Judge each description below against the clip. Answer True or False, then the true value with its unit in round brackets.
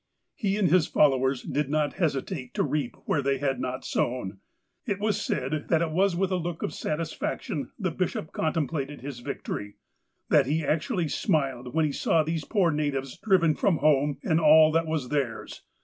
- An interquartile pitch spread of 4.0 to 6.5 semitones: False (3.5 semitones)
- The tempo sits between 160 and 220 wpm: True (180 wpm)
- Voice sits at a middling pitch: True (155 Hz)